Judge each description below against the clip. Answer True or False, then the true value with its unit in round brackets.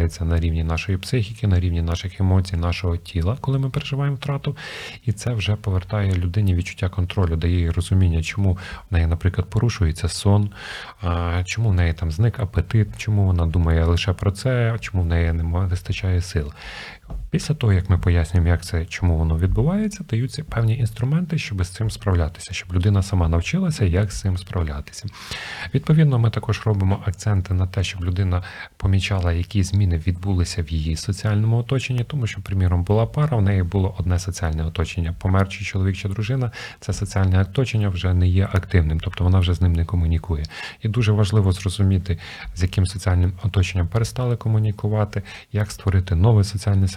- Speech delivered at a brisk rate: True (170 wpm)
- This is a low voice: True (95 Hz)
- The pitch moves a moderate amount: True (3.3 semitones)